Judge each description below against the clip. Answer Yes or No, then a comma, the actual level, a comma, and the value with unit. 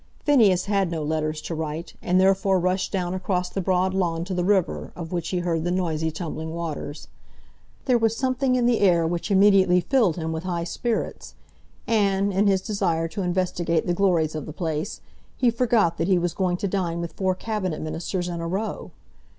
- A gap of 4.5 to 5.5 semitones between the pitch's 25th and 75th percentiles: No, average, 2.9 semitones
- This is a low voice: No, medium, 180 Hz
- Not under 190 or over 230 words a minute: Yes, average, 200 wpm